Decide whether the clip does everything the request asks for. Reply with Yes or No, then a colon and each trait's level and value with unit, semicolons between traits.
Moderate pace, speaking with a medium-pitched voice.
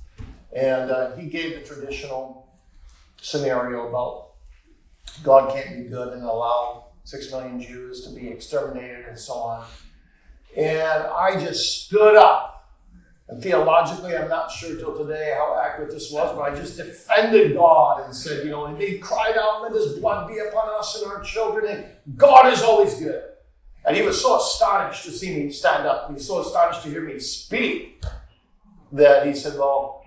Yes: average, 175 wpm; medium, 150 Hz